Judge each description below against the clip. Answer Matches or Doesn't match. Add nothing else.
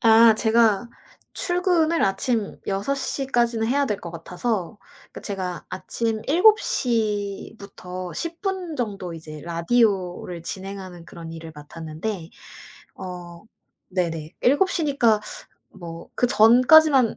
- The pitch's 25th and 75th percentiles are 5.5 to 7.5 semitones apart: Matches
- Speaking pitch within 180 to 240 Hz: Matches